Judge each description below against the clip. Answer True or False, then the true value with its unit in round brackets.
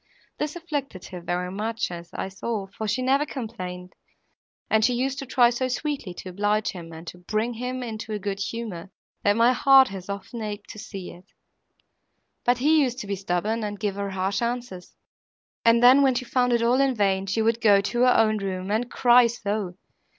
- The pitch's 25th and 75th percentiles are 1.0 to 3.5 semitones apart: False (4.1 semitones)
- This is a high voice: True (220 Hz)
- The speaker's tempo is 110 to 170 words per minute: False (205 wpm)